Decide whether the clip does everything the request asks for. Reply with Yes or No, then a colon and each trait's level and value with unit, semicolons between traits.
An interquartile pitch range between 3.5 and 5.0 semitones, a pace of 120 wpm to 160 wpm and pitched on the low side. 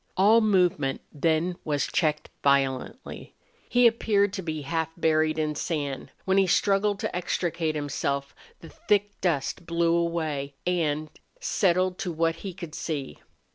No: average, 3.8 semitones; average, 140 wpm; medium, 165 Hz